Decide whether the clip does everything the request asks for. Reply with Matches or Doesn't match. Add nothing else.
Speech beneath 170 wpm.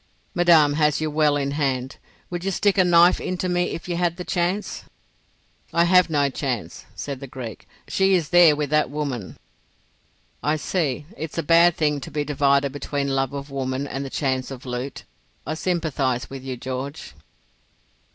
Doesn't match